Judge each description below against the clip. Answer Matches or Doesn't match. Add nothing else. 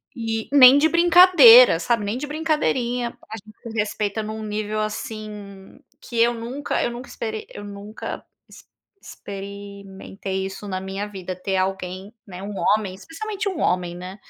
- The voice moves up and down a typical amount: Matches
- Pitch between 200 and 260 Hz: Matches